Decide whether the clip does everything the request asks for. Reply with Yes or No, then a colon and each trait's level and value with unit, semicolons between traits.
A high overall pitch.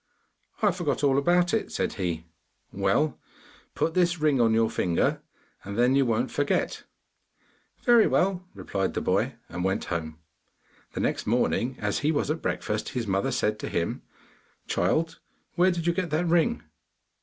No: low, 135 Hz